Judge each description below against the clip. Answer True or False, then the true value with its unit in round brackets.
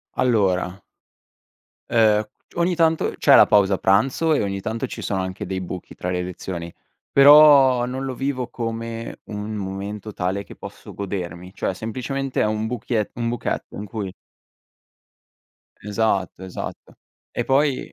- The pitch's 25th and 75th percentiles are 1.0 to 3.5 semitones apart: False (4.7 semitones)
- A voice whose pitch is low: True (110 Hz)